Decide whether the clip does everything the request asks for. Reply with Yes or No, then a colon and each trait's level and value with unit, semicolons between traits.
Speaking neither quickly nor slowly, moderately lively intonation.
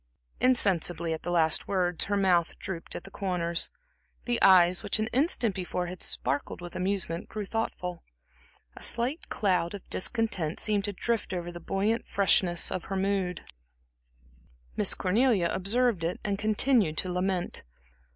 Yes: average, 150 wpm; average, 3.2 semitones